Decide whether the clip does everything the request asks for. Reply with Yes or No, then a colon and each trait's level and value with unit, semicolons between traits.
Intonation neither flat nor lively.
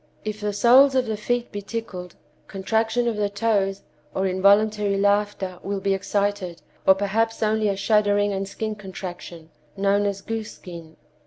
No: narrow, 2.0 semitones